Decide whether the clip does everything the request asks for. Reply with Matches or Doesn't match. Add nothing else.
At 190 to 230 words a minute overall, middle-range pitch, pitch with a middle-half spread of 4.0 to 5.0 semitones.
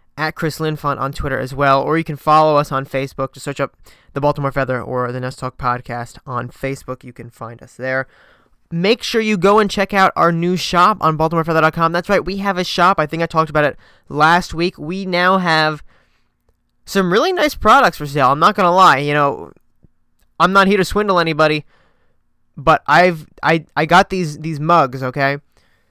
Matches